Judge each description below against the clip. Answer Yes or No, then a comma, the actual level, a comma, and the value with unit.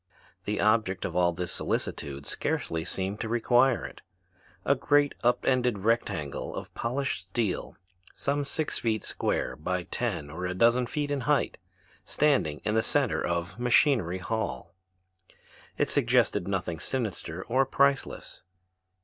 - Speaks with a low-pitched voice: Yes, low, 110 Hz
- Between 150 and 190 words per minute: No, average, 140 wpm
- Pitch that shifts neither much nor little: No, wide, 6.2 semitones